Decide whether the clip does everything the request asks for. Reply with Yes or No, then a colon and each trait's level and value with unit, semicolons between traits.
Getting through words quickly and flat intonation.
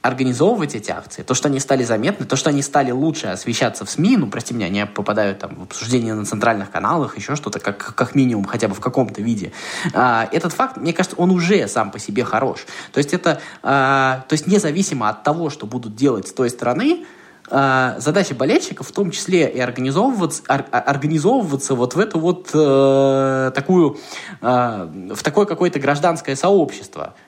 No: fast, 175 wpm; average, 5.2 semitones